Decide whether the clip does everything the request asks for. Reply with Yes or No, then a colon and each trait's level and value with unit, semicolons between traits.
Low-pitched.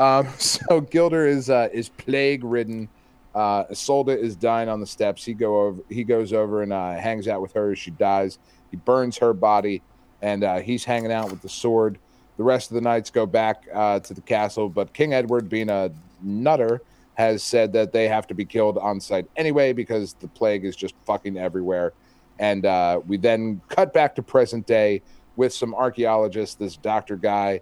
Yes: low, 110 Hz